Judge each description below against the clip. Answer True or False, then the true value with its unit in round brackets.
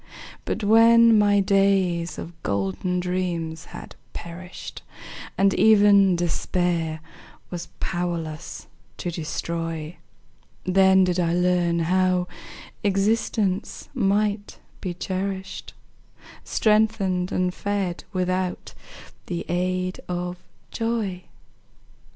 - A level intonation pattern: True (2.3 semitones)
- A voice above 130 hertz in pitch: True (185 Hz)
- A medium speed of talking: False (90 wpm)